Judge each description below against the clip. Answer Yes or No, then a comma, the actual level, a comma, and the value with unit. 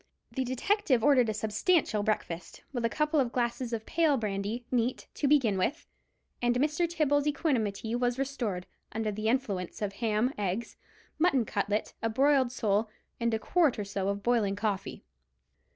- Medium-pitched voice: No, high, 235 Hz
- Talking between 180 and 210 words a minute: No, average, 165 wpm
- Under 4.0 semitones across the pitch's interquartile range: No, average, 4.5 semitones